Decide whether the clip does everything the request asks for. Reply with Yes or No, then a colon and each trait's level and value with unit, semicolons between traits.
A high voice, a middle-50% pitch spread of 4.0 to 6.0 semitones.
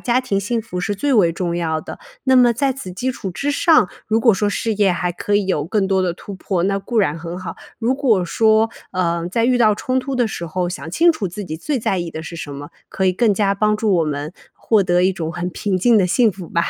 Yes: high, 195 Hz; average, 4.5 semitones